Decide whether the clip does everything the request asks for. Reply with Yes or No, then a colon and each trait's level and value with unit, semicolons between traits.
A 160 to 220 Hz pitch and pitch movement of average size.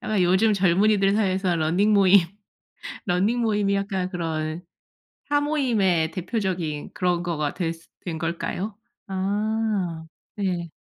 Yes: high, 190 Hz; average, 3.4 semitones